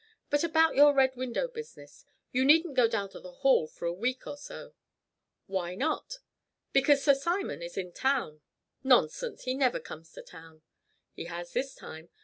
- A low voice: No, very high, 260 Hz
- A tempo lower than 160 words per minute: No, average, 175 wpm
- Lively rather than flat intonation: Yes, wide, 8.4 semitones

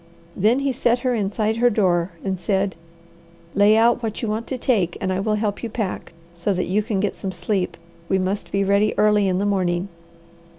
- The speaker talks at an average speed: No, fast, 210 wpm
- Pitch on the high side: Yes, high, 205 Hz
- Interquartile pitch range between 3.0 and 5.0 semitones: No, narrow, 2.6 semitones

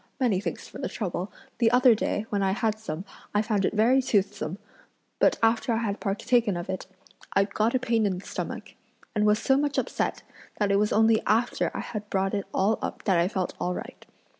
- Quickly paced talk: Yes, fast, 215 wpm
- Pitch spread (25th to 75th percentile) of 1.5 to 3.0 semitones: Yes, average, 2.7 semitones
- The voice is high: Yes, high, 210 Hz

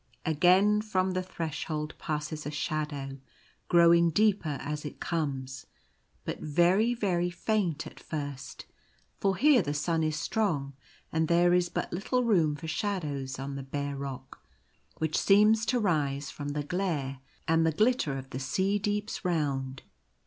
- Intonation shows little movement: No, average, 4.7 semitones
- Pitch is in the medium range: Yes, medium, 160 Hz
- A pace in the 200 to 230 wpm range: No, average, 150 wpm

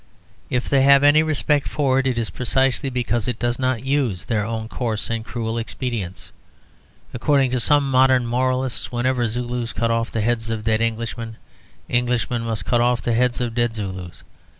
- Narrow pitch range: Yes, narrow, 2.2 semitones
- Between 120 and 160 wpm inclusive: No, average, 180 wpm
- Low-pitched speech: Yes, low, 120 Hz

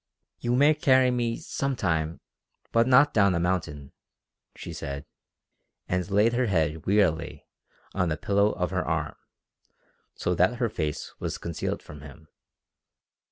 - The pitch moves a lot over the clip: Yes, wide, 6.8 semitones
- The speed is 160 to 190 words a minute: No, average, 145 wpm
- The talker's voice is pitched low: Yes, very low, 95 Hz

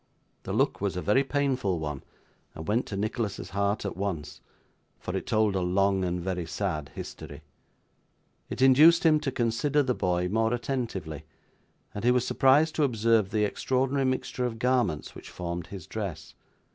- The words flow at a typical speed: Yes, average, 170 wpm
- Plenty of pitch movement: Yes, wide, 6.0 semitones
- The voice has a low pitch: Yes, low, 105 Hz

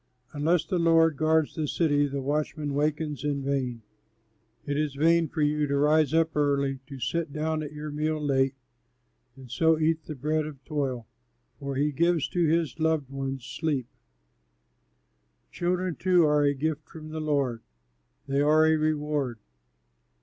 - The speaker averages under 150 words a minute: No, average, 160 wpm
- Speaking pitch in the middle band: Yes, medium, 150 Hz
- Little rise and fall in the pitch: Yes, narrow, 2.1 semitones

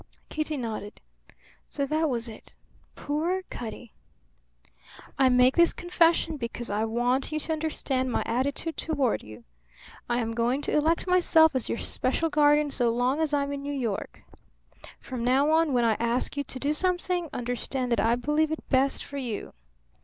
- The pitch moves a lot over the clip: No, average, 4.3 semitones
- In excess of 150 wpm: Yes, average, 170 wpm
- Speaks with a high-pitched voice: Yes, very high, 275 Hz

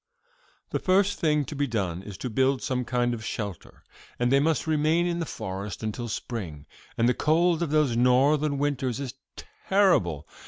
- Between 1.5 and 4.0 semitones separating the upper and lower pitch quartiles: No, average, 5.2 semitones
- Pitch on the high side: No, low, 130 Hz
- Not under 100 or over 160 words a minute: No, average, 180 wpm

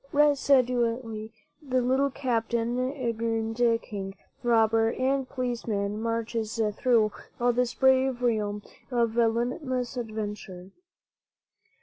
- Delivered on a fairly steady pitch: Yes, narrow, 2.3 semitones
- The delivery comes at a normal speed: No, slow, 95 wpm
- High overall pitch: Yes, high, 235 Hz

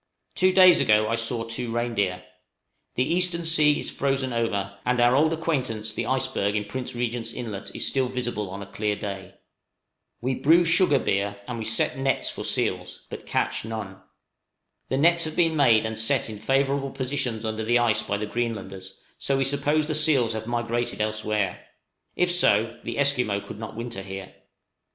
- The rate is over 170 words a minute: Yes, average, 185 wpm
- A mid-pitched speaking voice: No, low, 120 Hz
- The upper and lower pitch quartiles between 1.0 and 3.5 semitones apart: No, average, 4.3 semitones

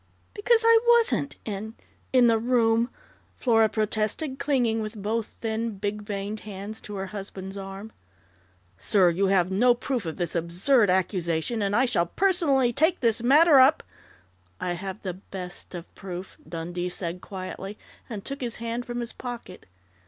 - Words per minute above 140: Yes, average, 160 wpm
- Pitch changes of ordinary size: Yes, average, 4.3 semitones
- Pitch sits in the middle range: No, high, 215 Hz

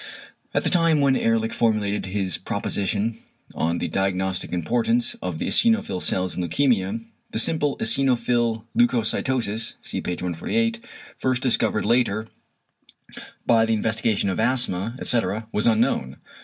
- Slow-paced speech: Yes, slow, 130 wpm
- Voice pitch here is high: No, low, 115 Hz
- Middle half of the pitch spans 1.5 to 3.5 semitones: No, average, 4.1 semitones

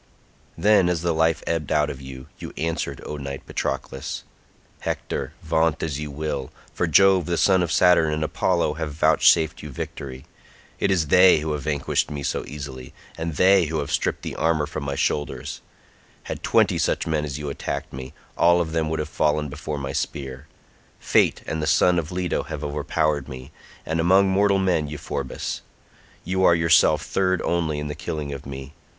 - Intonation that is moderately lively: Yes, average, 3.0 semitones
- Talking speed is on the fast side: No, average, 185 wpm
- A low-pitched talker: Yes, very low, 75 Hz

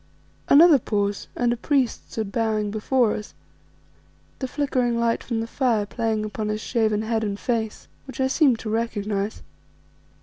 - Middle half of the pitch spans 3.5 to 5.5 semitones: No, narrow, 2.6 semitones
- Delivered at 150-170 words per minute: Yes, average, 160 wpm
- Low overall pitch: No, high, 225 Hz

